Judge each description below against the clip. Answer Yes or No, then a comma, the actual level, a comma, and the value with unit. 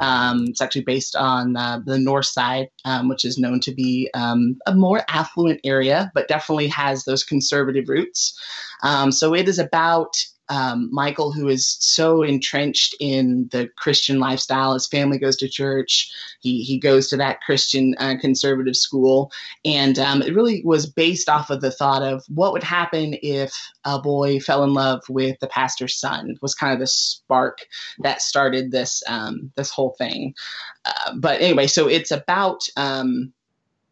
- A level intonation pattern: Yes, narrow, 1.9 semitones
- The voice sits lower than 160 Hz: Yes, low, 135 Hz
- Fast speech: No, average, 175 wpm